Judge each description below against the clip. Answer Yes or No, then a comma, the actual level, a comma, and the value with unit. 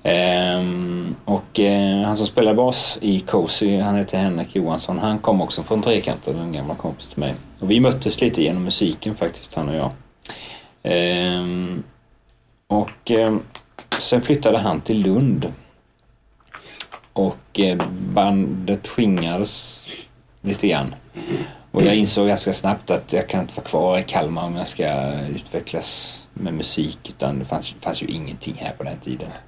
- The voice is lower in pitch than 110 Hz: Yes, low, 100 Hz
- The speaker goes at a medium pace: Yes, average, 155 wpm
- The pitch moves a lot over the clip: No, average, 3.1 semitones